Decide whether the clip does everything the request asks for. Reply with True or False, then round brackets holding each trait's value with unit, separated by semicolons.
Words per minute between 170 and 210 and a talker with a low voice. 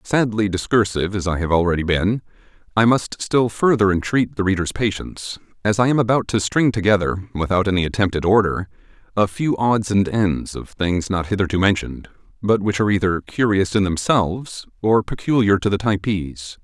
True (175 wpm; 100 Hz)